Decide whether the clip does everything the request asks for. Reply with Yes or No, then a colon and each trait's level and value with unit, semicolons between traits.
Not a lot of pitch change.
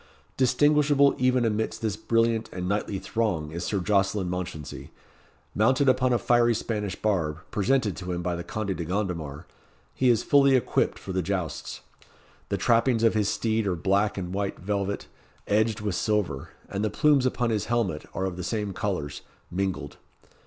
No: average, 4.1 semitones